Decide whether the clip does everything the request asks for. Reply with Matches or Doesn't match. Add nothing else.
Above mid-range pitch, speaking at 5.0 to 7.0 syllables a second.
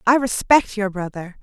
Doesn't match